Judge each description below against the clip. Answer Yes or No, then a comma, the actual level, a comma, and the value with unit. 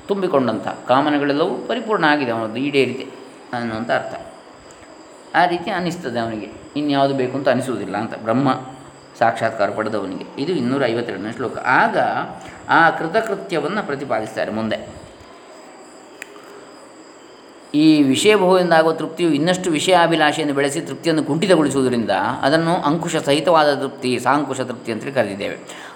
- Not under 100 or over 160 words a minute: Yes, fast, 105 wpm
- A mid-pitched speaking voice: Yes, medium, 150 Hz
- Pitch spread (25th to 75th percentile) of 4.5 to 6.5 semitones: Yes, average, 5.1 semitones